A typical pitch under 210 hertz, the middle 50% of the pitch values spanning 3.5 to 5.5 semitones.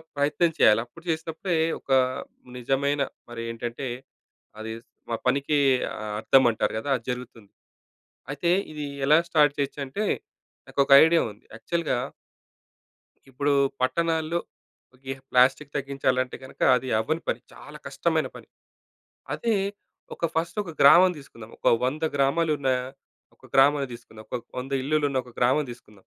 Yes: medium, 140 Hz; average, 4.0 semitones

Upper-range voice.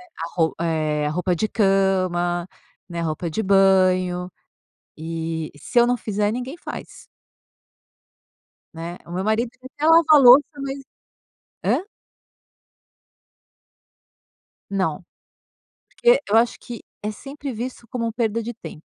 Yes: high, 195 Hz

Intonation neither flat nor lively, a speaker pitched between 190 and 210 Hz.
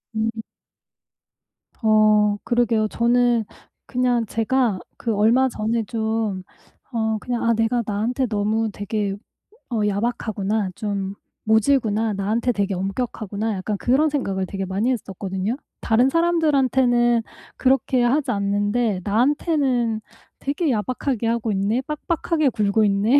No: average, 3.1 semitones; high, 225 Hz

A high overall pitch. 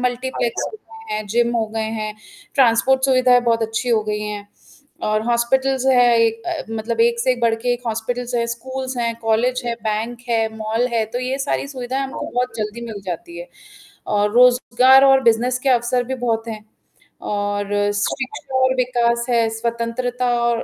Yes: high, 235 Hz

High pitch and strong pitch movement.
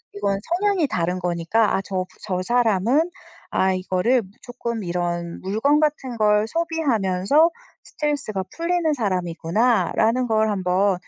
Yes: high, 215 Hz; wide, 6.5 semitones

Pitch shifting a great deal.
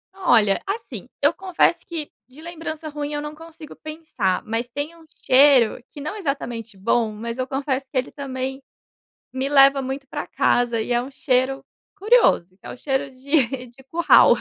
No: average, 3.8 semitones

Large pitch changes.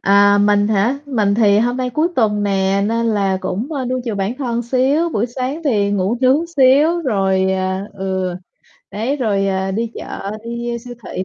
No: average, 4.4 semitones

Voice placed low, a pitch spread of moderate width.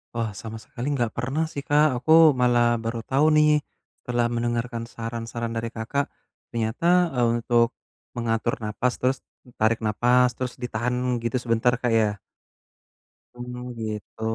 No: low, 120 Hz; narrow, 1.7 semitones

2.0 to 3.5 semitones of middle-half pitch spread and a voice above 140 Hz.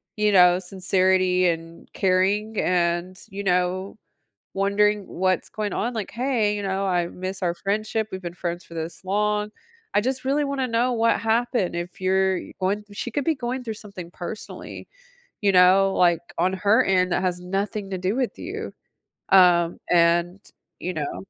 Yes: average, 2.7 semitones; high, 190 Hz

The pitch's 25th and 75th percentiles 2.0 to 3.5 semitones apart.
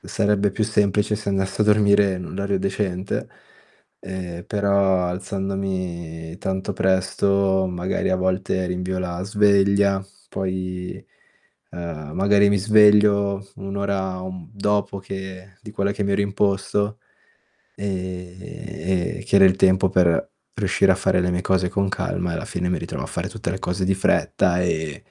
No: narrow, 1.6 semitones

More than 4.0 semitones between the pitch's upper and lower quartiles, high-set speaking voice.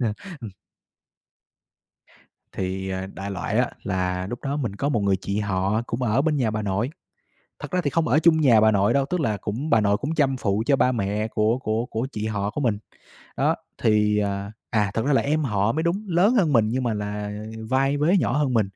No: average, 5.3 semitones; low, 110 Hz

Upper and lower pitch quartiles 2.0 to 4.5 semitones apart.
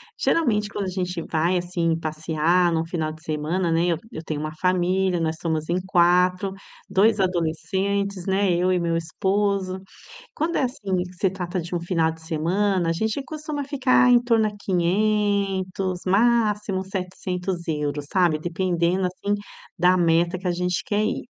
Yes: average, 2.9 semitones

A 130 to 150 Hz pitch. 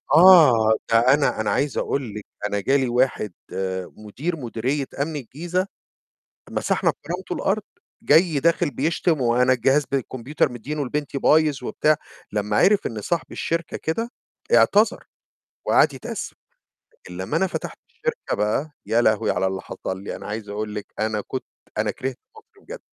Yes: low, 135 Hz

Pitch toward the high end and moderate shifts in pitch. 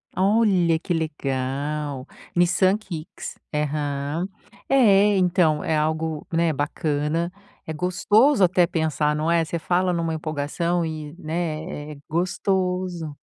No: medium, 165 Hz; average, 3.1 semitones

